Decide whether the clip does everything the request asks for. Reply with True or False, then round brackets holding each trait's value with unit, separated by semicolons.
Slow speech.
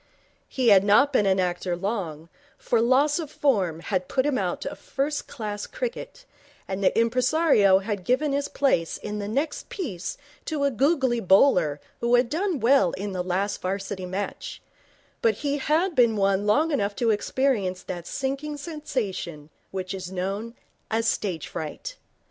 False (165 wpm)